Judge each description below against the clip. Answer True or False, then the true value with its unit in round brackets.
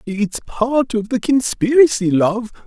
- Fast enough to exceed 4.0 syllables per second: False (3.8 syllables/s)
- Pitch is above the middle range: True (230 Hz)